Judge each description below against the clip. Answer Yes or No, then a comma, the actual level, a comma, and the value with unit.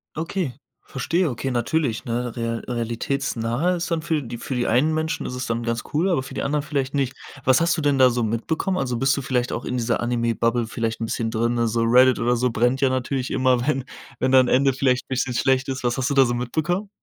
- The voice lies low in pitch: Yes, low, 125 Hz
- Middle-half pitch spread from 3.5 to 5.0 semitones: No, average, 2.7 semitones